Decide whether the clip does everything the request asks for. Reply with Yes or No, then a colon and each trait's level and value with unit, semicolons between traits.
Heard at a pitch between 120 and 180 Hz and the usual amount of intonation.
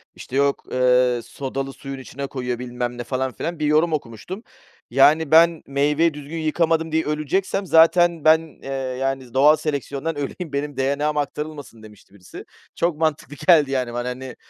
Yes: medium, 140 Hz; average, 3.4 semitones